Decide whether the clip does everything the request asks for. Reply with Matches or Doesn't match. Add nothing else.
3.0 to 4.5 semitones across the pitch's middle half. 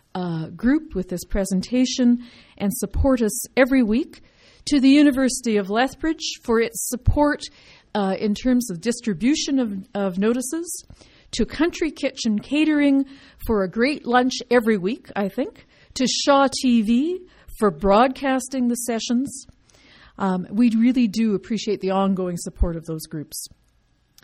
Doesn't match